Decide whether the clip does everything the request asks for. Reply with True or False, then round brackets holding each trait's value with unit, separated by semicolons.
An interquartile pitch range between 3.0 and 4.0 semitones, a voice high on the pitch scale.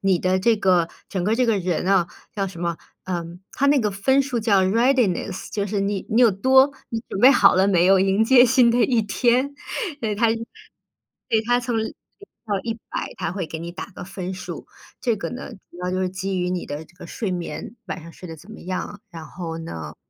False (4.4 semitones; 195 Hz)